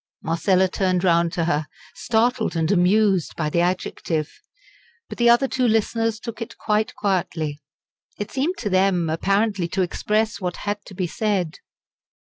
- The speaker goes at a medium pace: Yes, average, 155 wpm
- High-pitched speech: Yes, high, 195 Hz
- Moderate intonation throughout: Yes, average, 4.1 semitones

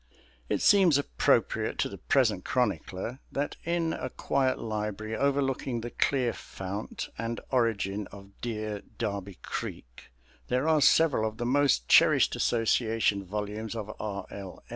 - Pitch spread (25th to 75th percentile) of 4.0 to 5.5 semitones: Yes, average, 4.5 semitones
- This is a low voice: Yes, low, 115 Hz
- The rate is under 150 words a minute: Yes, average, 140 wpm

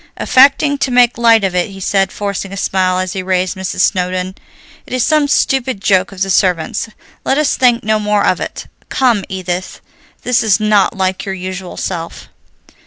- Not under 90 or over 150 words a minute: No, average, 185 wpm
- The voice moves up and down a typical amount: Yes, average, 4.1 semitones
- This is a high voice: Yes, high, 195 Hz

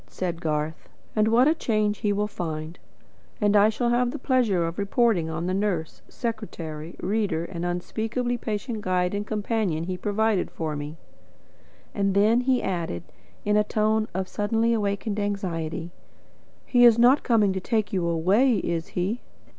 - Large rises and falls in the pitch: No, average, 4.3 semitones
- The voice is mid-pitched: No, high, 205 Hz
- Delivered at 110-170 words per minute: Yes, average, 160 wpm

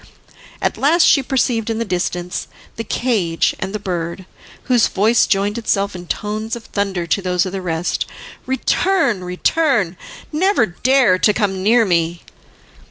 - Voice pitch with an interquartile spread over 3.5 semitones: Yes, average, 4.7 semitones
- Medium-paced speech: Yes, average, 155 wpm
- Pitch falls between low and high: No, high, 205 Hz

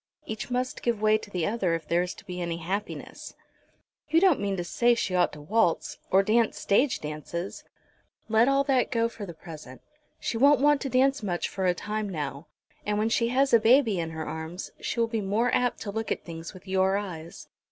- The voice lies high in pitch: Yes, high, 205 Hz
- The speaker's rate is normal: No, fast, 220 wpm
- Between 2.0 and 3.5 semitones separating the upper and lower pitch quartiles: No, average, 5.2 semitones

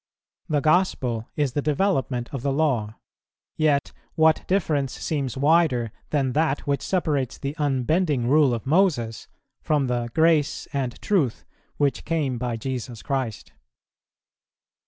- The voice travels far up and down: No, average, 3.8 semitones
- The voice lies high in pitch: No, medium, 140 Hz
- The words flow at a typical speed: No, slow, 130 wpm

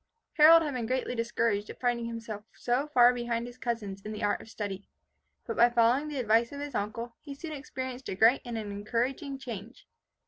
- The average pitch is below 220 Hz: No, high, 235 Hz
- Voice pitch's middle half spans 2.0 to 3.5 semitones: Yes, average, 2.7 semitones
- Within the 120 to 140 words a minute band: No, fast, 205 wpm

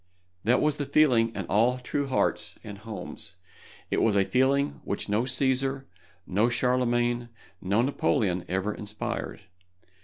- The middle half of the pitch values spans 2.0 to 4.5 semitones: Yes, average, 4.0 semitones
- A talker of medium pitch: No, low, 120 Hz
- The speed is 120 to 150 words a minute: Yes, average, 140 wpm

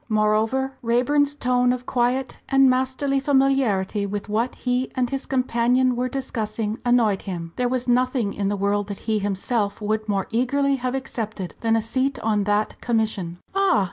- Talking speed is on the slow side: No, average, 170 wpm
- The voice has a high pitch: Yes, high, 240 Hz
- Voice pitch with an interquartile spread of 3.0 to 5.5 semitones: Yes, average, 3.5 semitones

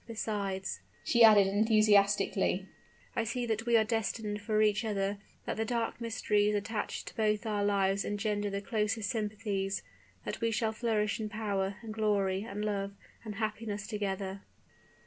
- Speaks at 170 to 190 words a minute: No, average, 155 wpm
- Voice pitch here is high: Yes, high, 210 Hz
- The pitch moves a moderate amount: No, narrow, 1.7 semitones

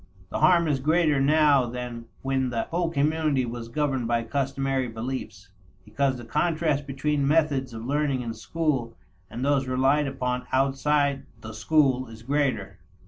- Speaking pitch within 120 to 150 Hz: Yes, low, 135 Hz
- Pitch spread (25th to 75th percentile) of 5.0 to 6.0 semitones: No, average, 3.2 semitones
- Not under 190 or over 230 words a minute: No, average, 150 wpm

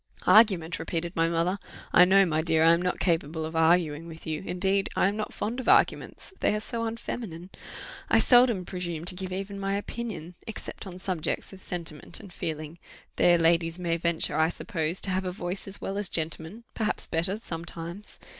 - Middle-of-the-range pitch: Yes, medium, 180 Hz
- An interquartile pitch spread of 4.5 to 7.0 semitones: No, average, 3.0 semitones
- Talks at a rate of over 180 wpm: Yes, average, 190 wpm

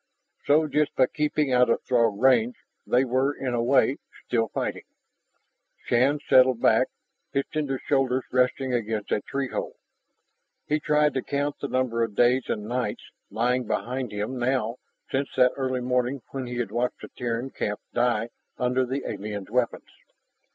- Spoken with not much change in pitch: Yes, narrow, 2.3 semitones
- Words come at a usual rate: Yes, average, 165 wpm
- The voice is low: Yes, low, 125 Hz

